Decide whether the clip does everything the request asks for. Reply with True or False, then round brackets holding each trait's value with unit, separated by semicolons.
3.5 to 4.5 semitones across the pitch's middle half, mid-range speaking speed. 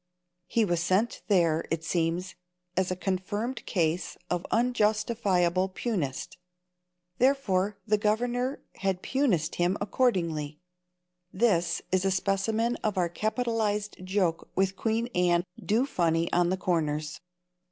False (4.1 semitones; 120 wpm)